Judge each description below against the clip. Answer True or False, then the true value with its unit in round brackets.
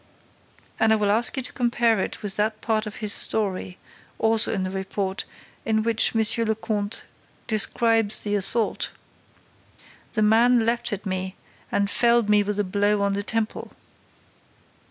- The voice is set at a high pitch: True (215 Hz)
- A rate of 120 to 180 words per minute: True (160 wpm)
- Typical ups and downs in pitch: False (1.9 semitones)